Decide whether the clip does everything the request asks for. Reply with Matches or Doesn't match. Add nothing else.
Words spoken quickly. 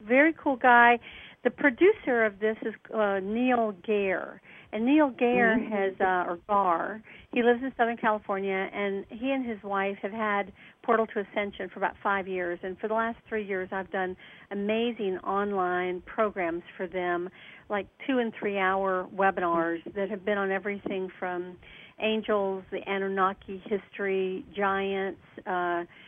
Doesn't match